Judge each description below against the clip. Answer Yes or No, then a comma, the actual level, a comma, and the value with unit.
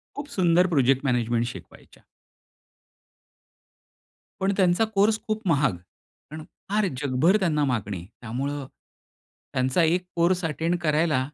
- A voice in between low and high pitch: Yes, medium, 155 Hz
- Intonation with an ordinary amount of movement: No, wide, 5.8 semitones